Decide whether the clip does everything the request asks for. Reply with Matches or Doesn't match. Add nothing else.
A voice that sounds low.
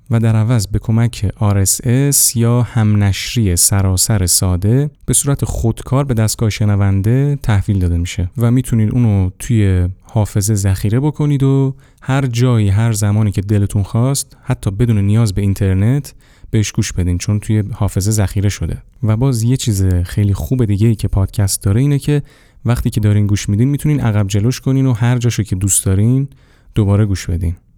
Matches